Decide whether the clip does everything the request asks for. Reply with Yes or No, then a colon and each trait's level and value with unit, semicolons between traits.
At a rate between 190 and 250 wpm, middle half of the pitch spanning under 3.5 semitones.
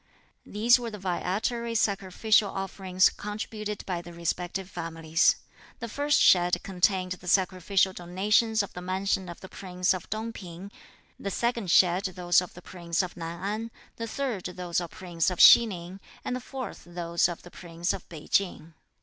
No: average, 175 wpm; average, 3.1 semitones